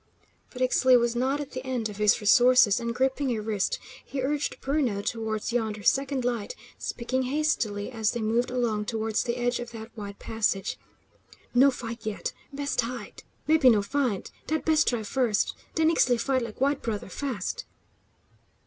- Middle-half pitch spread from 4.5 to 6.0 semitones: No, average, 3.3 semitones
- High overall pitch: Yes, high, 240 Hz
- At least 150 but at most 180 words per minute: Yes, average, 170 wpm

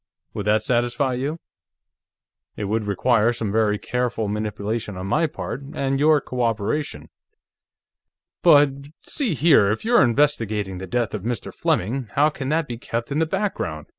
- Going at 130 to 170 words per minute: Yes, average, 155 wpm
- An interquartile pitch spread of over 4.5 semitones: Yes, wide, 5.4 semitones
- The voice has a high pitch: No, low, 120 Hz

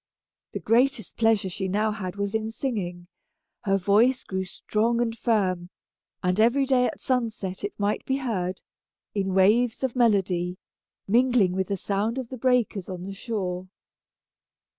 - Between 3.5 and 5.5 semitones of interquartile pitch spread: Yes, average, 4.1 semitones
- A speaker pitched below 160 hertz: No, high, 210 Hz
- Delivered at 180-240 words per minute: No, average, 155 wpm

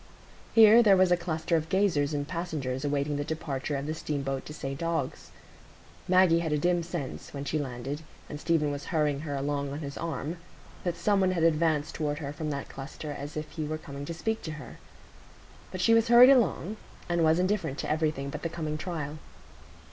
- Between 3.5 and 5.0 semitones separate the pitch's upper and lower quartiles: No, average, 3.1 semitones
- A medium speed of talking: No, fast, 210 wpm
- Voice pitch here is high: No, medium, 155 Hz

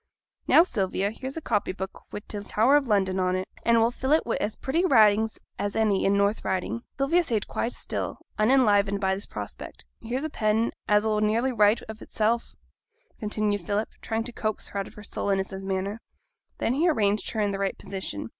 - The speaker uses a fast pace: Yes, fast, 210 wpm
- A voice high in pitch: Yes, high, 215 Hz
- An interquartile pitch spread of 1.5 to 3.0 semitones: Yes, average, 2.7 semitones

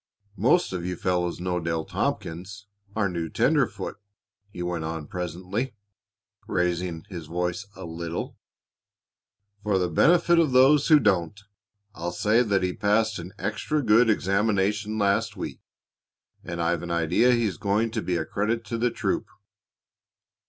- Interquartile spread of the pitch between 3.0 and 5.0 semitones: Yes, average, 4.2 semitones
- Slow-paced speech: No, average, 145 wpm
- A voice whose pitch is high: No, very low, 95 Hz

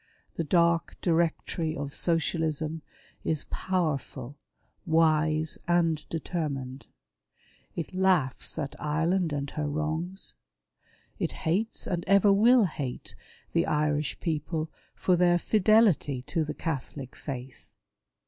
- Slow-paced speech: Yes, slow, 110 wpm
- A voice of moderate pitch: Yes, medium, 160 Hz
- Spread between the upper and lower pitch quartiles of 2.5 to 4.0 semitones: Yes, average, 2.8 semitones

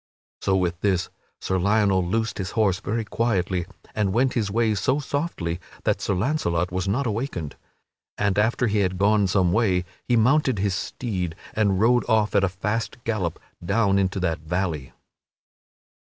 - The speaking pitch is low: Yes, low, 100 Hz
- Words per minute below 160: No, average, 165 wpm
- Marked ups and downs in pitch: No, average, 3.6 semitones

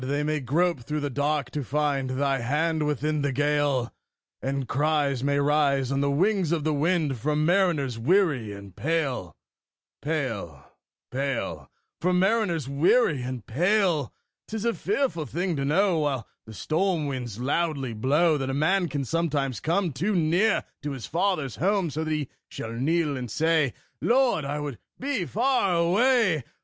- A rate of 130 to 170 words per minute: Yes, average, 160 wpm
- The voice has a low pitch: No, medium, 150 Hz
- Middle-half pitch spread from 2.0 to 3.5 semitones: No, average, 4.1 semitones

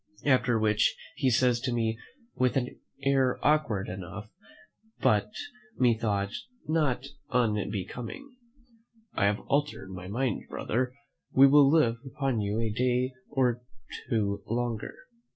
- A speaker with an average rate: No, slow, 120 wpm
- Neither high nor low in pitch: No, low, 120 Hz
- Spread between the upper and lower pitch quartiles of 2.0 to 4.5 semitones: Yes, average, 3.7 semitones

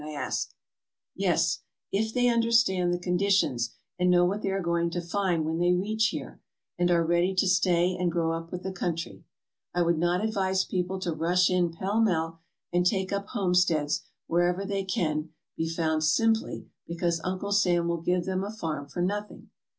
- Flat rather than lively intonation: Yes, narrow, 2.3 semitones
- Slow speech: No, average, 190 wpm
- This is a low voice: No, medium, 180 Hz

